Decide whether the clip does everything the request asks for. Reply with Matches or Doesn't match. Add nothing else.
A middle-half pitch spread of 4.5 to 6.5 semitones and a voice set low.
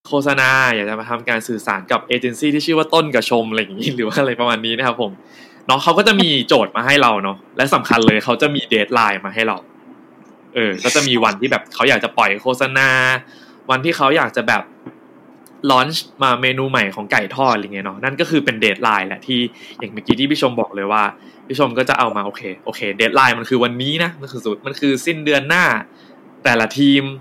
Doesn't match